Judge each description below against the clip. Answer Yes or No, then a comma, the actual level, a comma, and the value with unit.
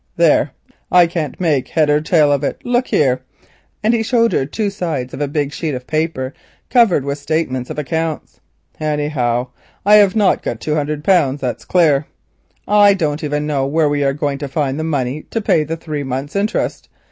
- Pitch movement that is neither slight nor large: Yes, average, 3.4 semitones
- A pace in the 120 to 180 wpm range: No, average, 195 wpm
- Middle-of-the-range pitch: Yes, medium, 150 Hz